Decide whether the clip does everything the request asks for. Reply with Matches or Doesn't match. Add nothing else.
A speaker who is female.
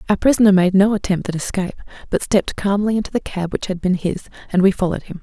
Matches